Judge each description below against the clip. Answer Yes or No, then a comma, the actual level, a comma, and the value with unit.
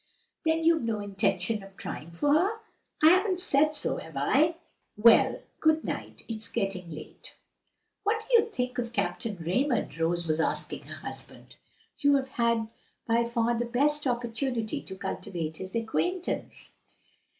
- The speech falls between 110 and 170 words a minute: Yes, average, 150 wpm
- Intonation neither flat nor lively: No, wide, 7.4 semitones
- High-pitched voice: Yes, high, 235 Hz